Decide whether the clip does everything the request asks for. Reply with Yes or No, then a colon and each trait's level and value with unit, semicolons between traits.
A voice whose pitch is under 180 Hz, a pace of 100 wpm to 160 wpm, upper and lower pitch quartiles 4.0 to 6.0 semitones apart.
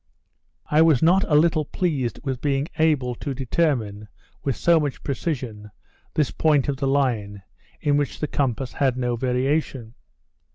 No: low, 135 Hz; average, 155 wpm; average, 3.4 semitones